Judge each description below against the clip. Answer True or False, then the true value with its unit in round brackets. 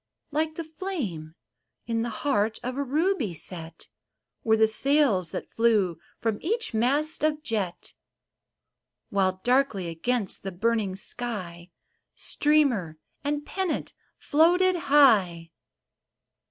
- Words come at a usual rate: False (115 wpm)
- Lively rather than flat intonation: True (7.8 semitones)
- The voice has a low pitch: False (230 Hz)